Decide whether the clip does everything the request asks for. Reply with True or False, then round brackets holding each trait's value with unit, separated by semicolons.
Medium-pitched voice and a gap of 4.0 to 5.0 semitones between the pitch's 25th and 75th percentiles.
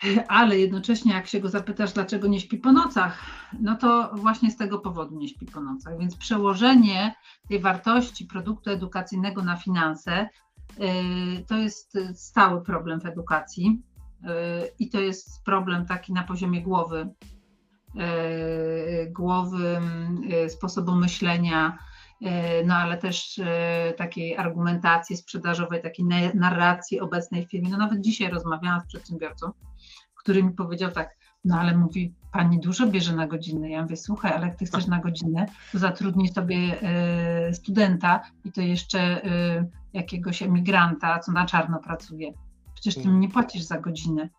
False (180 Hz; 2.6 semitones)